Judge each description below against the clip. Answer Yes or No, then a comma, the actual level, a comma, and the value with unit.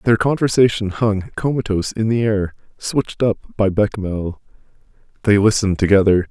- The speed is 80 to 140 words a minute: Yes, slow, 135 wpm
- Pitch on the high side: No, low, 105 Hz